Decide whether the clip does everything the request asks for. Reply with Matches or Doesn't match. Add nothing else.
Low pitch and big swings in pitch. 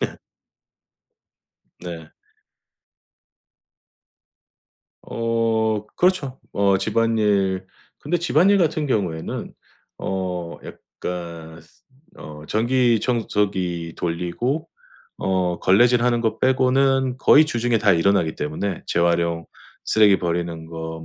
Matches